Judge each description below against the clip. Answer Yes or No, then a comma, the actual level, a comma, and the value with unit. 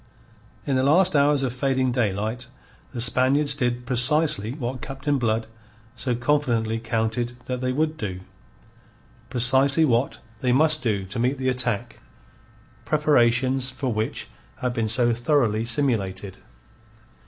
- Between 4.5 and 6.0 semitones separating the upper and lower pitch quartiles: No, average, 3.0 semitones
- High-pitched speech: No, low, 125 Hz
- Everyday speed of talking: No, slow, 130 wpm